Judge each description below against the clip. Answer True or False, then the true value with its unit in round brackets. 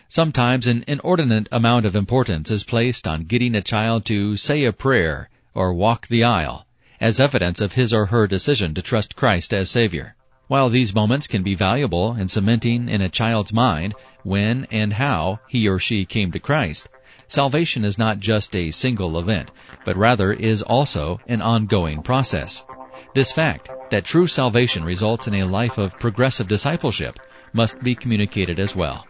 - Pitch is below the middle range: True (115 Hz)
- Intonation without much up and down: False (4.4 semitones)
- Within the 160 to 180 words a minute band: True (175 wpm)